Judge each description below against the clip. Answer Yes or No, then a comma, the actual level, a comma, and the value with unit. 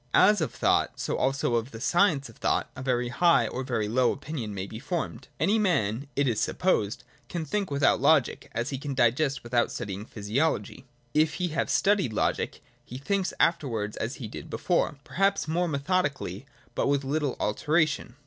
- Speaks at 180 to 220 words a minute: Yes, average, 185 wpm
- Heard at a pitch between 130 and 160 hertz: Yes, medium, 140 Hz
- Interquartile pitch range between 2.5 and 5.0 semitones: No, wide, 5.4 semitones